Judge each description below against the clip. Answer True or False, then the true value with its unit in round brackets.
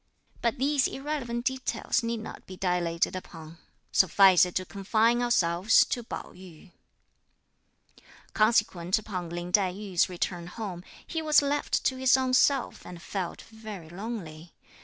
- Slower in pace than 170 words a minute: True (140 wpm)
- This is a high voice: True (200 Hz)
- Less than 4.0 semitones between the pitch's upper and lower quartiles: False (5.3 semitones)